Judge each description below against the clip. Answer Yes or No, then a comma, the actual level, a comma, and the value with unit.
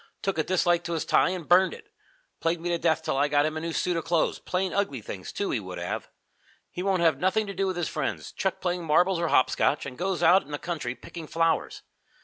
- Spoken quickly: Yes, fast, 250 wpm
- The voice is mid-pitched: Yes, medium, 170 Hz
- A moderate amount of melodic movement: Yes, average, 3.1 semitones